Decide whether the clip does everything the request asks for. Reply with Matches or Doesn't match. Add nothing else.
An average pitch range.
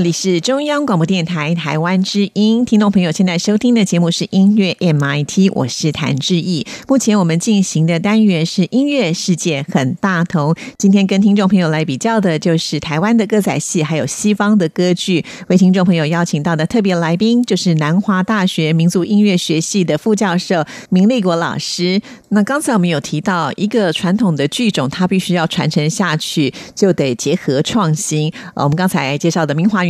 Matches